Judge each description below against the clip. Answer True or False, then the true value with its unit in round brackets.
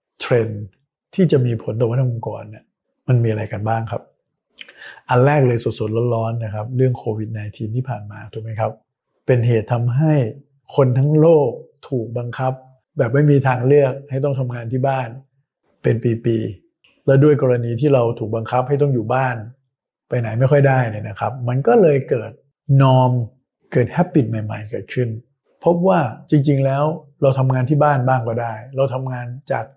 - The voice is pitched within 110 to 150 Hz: True (130 Hz)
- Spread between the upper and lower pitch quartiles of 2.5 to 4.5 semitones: True (3.2 semitones)